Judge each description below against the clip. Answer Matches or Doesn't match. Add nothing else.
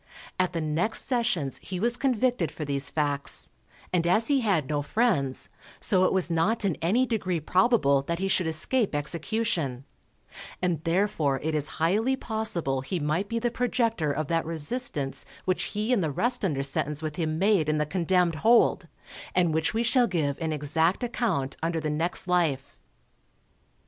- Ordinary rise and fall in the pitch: Doesn't match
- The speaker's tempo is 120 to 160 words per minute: Doesn't match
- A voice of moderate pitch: Matches